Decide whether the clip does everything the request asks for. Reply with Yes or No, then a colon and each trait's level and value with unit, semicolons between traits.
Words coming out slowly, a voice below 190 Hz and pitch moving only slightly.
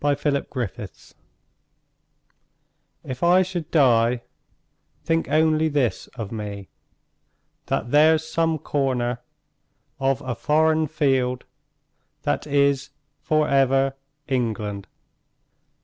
No: slow, 95 wpm; medium, 140 Hz; average, 4.0 semitones